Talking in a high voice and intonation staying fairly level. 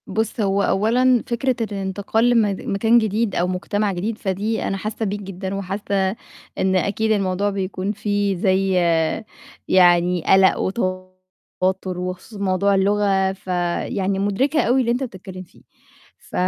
Yes: high, 195 Hz; narrow, 2.3 semitones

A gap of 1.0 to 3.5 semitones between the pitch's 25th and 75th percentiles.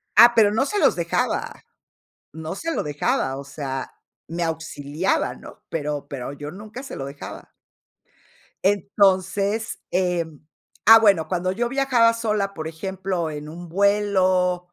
No: average, 4.7 semitones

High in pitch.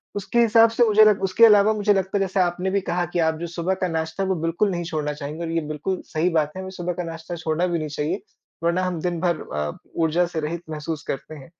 No: medium, 175 Hz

